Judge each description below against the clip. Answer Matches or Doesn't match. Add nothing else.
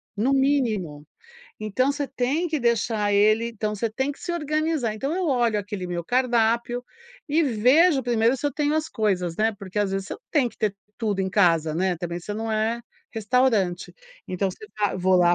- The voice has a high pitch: Matches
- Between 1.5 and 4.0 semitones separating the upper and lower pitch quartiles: Doesn't match